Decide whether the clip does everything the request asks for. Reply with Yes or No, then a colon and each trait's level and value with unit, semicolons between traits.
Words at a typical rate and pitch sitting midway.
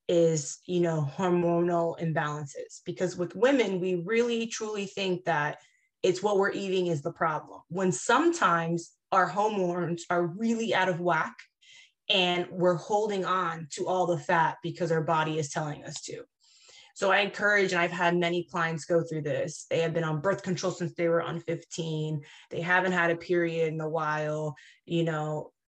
Yes: average, 175 wpm; medium, 175 Hz